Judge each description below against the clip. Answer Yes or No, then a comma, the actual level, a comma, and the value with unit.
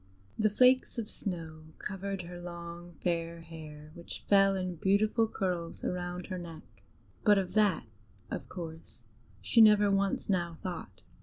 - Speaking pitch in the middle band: Yes, medium, 180 Hz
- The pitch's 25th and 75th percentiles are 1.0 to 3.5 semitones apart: Yes, average, 2.9 semitones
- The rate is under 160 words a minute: Yes, average, 145 wpm